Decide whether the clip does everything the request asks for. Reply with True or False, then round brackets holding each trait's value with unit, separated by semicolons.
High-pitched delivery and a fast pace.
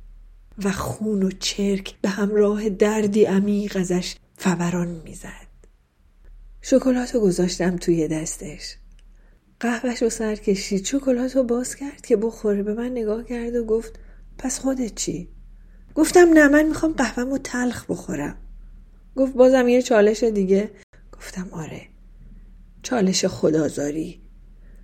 False (205 Hz; 125 wpm)